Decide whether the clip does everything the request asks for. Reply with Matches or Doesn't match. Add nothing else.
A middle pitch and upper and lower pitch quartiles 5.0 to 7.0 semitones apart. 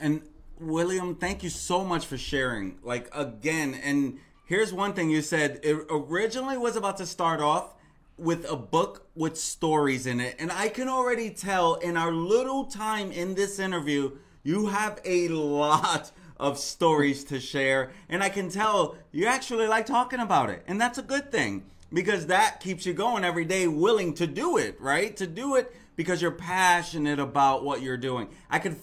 Matches